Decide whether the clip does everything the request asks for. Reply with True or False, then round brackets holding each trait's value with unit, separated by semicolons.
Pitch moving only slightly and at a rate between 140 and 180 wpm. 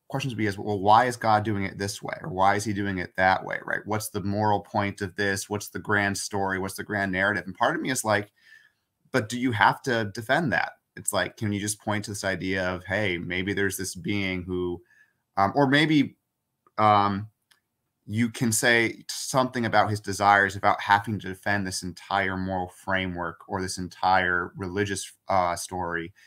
False (2.2 semitones; 205 wpm)